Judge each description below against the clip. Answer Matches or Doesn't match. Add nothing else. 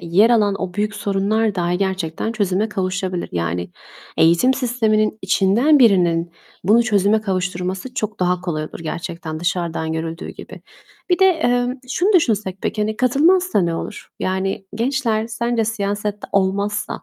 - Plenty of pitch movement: Doesn't match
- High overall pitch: Matches